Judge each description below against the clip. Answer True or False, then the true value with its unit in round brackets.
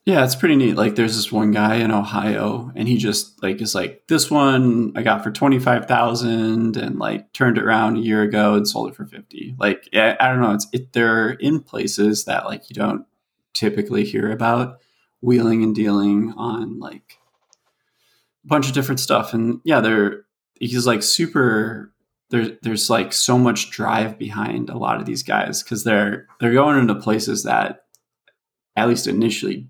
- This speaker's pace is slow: False (185 wpm)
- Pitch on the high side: False (115 Hz)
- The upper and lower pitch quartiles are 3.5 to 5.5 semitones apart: False (2.4 semitones)